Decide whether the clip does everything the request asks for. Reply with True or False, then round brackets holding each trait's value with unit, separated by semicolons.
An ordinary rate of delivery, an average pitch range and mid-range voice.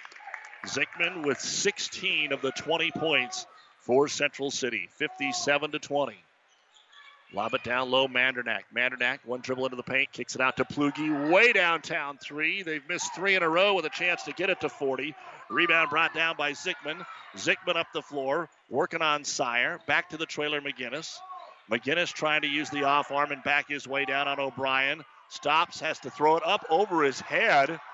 True (185 wpm; 3.3 semitones; 145 Hz)